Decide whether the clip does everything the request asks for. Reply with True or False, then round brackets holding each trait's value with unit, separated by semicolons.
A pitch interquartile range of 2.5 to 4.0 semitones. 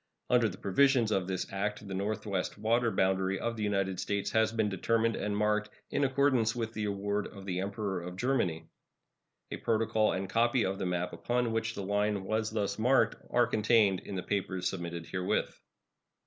True (2.8 semitones)